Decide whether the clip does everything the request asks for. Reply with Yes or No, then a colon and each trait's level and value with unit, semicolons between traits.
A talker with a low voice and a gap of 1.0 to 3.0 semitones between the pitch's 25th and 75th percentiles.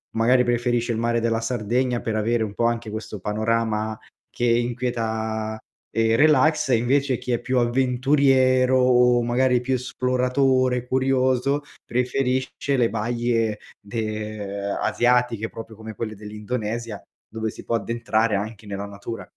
Yes: low, 120 Hz; narrow, 2.5 semitones